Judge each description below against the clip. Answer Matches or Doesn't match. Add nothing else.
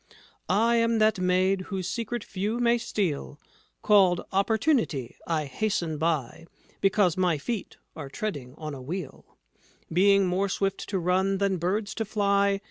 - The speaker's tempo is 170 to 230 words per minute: Doesn't match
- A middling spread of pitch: Matches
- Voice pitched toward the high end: Matches